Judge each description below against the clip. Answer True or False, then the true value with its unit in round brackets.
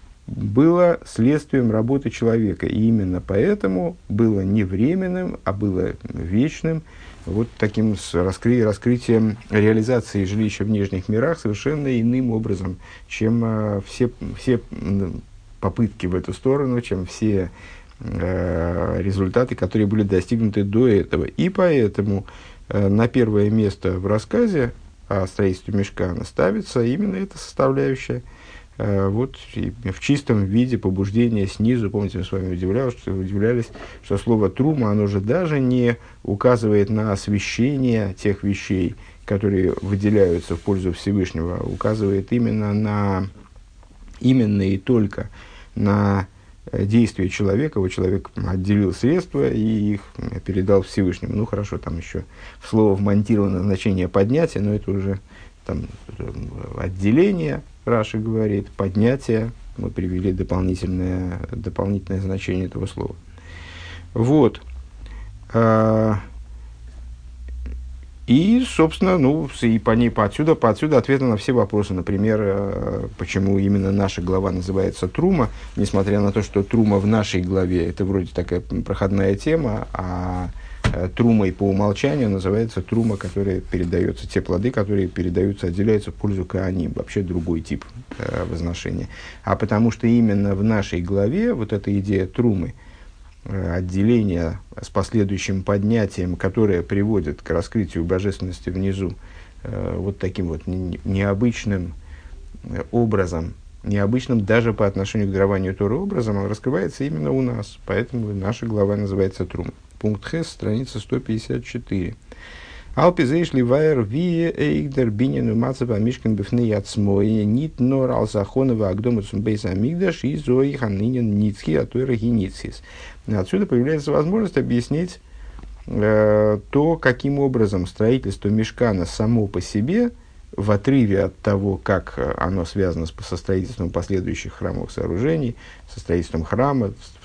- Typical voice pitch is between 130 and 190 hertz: False (100 Hz)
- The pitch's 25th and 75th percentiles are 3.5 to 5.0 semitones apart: True (3.8 semitones)